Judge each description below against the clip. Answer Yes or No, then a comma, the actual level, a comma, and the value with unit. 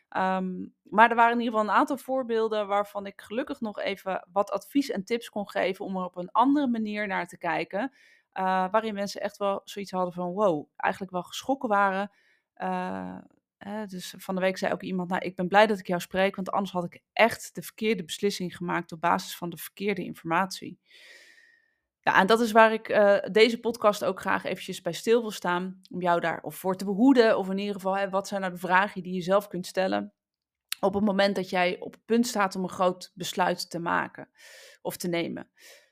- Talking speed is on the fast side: Yes, fast, 215 wpm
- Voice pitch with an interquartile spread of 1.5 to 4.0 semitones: Yes, average, 3.0 semitones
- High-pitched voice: Yes, high, 195 Hz